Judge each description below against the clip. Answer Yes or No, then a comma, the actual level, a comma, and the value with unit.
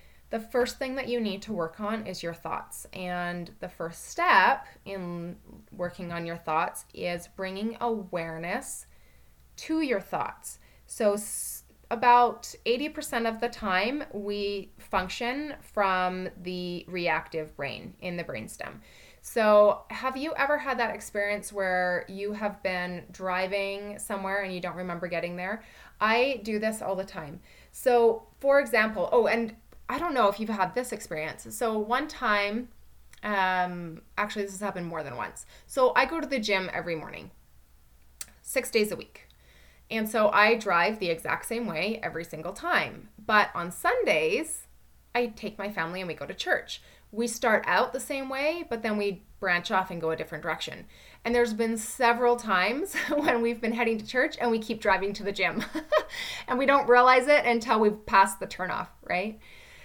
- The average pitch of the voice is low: No, high, 205 Hz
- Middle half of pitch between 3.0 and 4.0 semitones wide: No, average, 4.9 semitones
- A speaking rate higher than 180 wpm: No, average, 170 wpm